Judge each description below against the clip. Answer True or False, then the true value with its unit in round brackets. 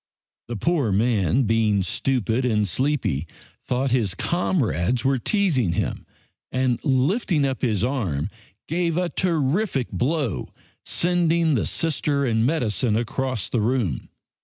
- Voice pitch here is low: True (130 Hz)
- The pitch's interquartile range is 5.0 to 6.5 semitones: True (5.6 semitones)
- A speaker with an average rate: False (125 wpm)